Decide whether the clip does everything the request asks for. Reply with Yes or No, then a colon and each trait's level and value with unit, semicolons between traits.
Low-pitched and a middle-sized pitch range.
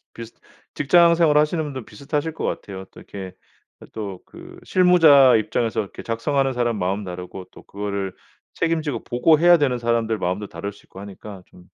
No: low, 115 Hz; wide, 6.8 semitones